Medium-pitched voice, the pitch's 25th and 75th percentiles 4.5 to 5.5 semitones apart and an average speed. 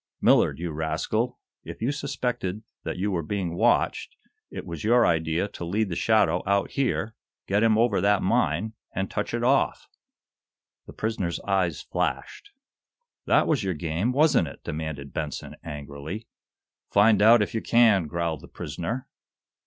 No: low, 100 Hz; average, 5.2 semitones; average, 155 wpm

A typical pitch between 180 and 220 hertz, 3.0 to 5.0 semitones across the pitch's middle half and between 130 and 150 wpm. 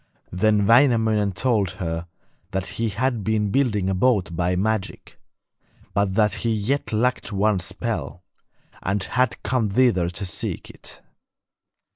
No: low, 105 Hz; average, 3.5 semitones; slow, 135 wpm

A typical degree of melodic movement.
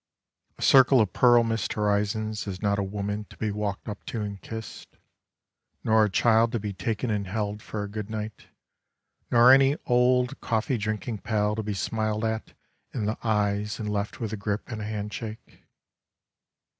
No: narrow, 1.5 semitones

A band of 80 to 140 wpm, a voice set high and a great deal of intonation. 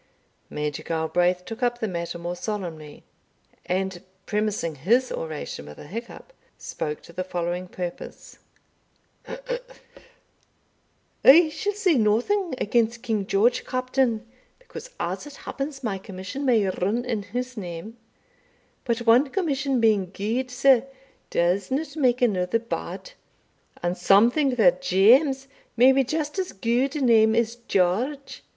Yes: slow, 135 wpm; high, 230 Hz; wide, 6.1 semitones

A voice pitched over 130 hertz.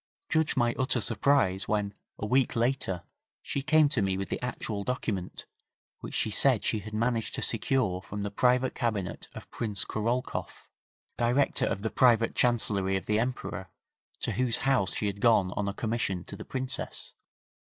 No: low, 115 Hz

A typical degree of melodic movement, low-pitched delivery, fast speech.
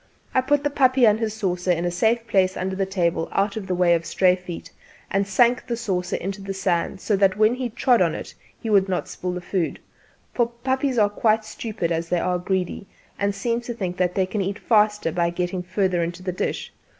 No: average, 3.6 semitones; high, 195 Hz; fast, 230 wpm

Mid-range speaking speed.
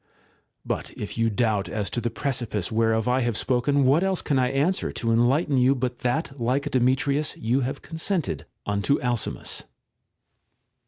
Yes: average, 165 wpm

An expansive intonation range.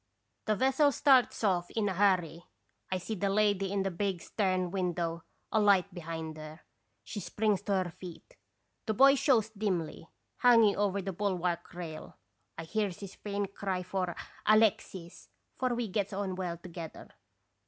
No: average, 3.1 semitones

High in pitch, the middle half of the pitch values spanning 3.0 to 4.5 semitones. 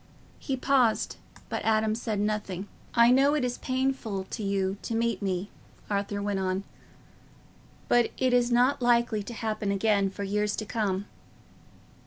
Yes: high, 215 Hz; average, 3.3 semitones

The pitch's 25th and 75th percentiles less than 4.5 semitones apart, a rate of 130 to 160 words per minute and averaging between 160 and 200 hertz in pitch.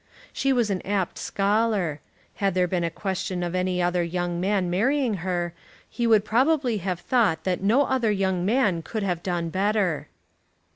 No: average, 3.7 semitones; average, 175 wpm; high, 190 Hz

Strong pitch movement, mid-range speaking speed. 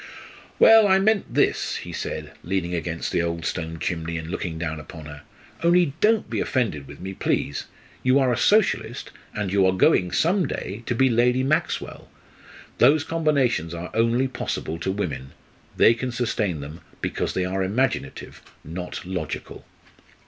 Yes: wide, 7.9 semitones; average, 165 wpm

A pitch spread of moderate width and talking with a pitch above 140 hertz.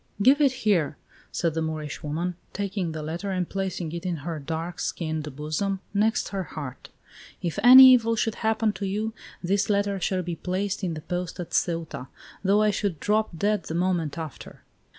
Yes: average, 4.1 semitones; medium, 185 Hz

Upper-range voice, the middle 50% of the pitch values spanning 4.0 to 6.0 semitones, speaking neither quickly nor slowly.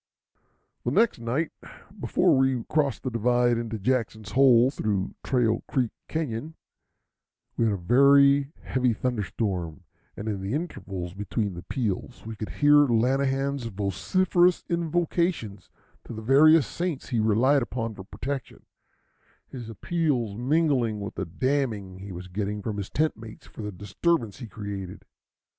No: low, 120 Hz; average, 5.1 semitones; average, 145 wpm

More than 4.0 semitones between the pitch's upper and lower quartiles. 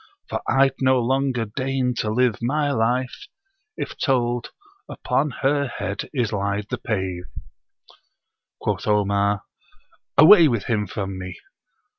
Yes: average, 4.6 semitones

